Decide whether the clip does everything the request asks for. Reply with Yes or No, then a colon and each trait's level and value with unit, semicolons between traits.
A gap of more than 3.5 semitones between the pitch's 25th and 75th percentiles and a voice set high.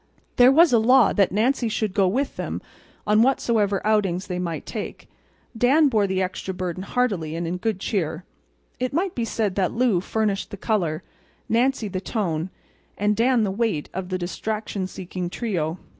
Yes: average, 4.1 semitones; high, 205 Hz